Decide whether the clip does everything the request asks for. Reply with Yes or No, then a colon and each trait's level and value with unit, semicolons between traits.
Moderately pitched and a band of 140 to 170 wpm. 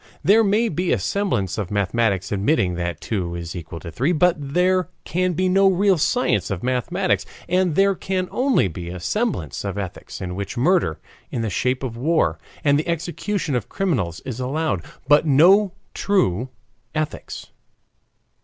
Yes: medium, 145 Hz; average, 165 wpm